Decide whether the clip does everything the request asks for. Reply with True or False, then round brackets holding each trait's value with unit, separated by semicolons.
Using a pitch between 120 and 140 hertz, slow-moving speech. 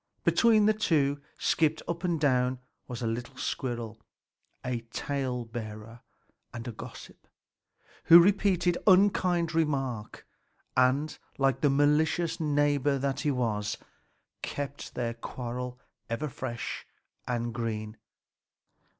True (135 Hz; 115 wpm)